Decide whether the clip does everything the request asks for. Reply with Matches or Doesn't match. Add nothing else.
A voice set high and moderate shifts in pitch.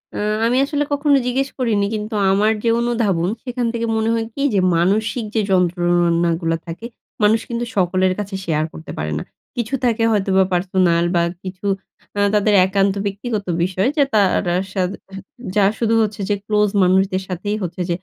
Matches